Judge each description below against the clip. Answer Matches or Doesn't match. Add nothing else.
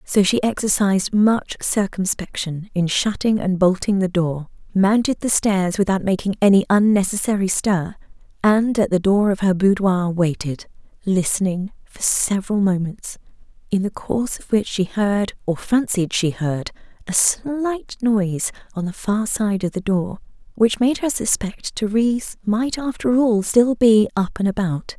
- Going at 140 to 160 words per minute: Matches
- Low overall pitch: Doesn't match